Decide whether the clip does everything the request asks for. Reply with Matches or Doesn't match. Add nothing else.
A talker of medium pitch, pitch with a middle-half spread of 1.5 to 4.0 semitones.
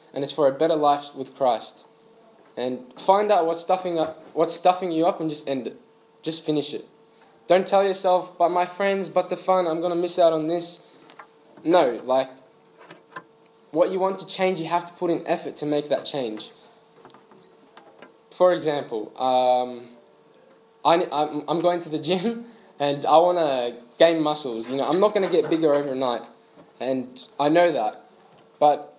Doesn't match